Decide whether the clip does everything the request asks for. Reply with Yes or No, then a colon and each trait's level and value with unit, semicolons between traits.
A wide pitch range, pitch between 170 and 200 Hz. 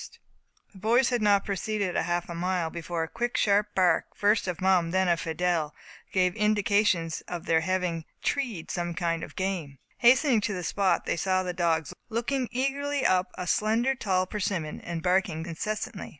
No: average, 3.8 semitones; medium, 185 Hz